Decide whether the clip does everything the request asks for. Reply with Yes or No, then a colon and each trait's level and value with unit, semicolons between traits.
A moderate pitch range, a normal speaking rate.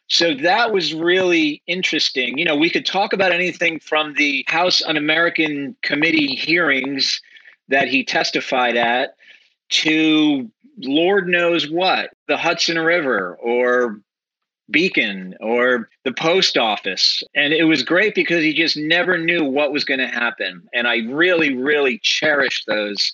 Yes: average, 4.1 semitones; average, 145 wpm